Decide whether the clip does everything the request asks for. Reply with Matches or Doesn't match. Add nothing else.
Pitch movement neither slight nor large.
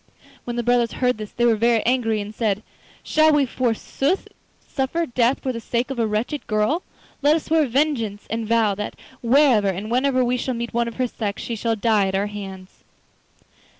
Matches